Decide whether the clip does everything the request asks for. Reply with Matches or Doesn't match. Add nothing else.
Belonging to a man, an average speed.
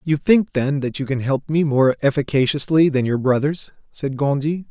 Matches